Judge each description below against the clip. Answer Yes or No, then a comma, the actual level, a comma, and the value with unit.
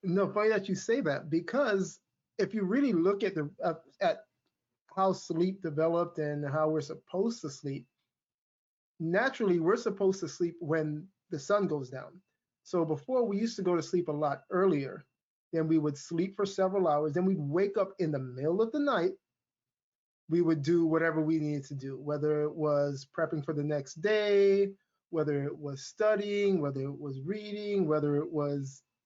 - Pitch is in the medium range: Yes, medium, 170 Hz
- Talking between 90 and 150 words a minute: No, average, 185 wpm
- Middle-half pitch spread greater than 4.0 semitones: Yes, average, 4.8 semitones